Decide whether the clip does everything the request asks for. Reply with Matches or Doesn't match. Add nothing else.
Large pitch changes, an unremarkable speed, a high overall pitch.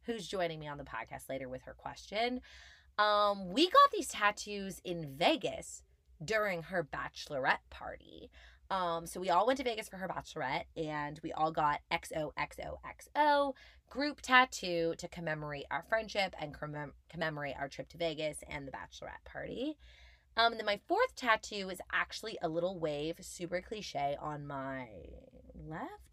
Doesn't match